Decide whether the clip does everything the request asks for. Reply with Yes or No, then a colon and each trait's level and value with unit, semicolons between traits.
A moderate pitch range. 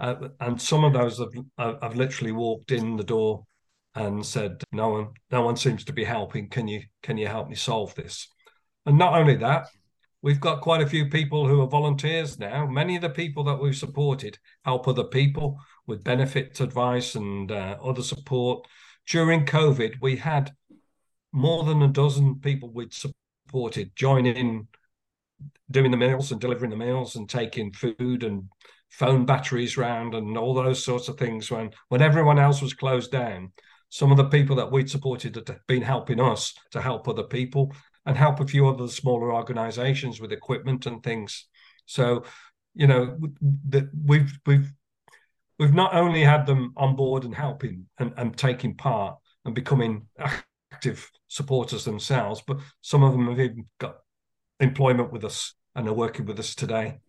Yes: average, 3.0 semitones